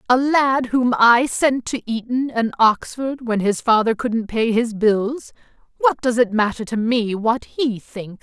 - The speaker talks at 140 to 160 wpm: No, average, 175 wpm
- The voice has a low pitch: No, high, 235 Hz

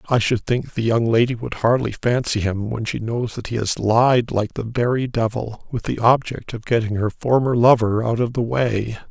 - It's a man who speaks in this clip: Yes, male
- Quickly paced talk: Yes, fast, 215 wpm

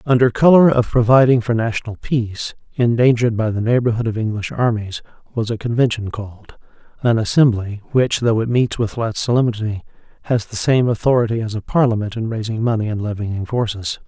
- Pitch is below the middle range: Yes, low, 115 Hz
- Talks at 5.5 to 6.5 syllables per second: Yes, 5.7 syllables/s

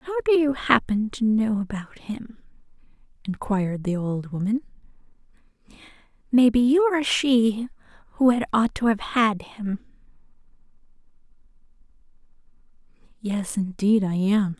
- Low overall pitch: No, high, 225 Hz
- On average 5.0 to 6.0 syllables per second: No, 4.5 syllables/s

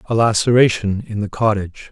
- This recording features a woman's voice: No, male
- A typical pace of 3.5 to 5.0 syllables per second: No, 5.6 syllables/s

